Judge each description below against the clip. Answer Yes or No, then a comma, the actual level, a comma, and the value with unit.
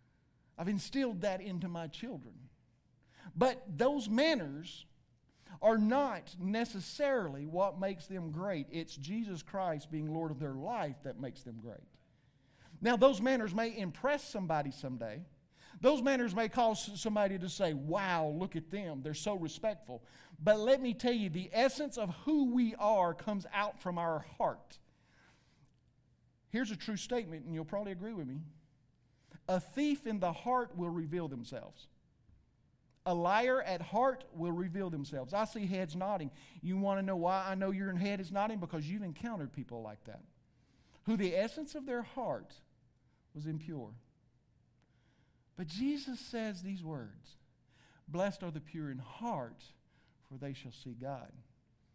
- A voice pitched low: No, medium, 180 Hz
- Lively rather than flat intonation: Yes, wide, 6.5 semitones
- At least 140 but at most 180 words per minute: Yes, average, 155 wpm